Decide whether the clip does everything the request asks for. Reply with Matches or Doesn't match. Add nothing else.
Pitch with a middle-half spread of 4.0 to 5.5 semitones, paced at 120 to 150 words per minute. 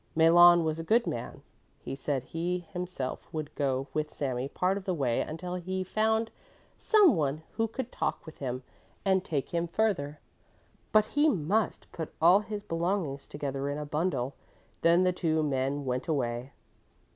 Doesn't match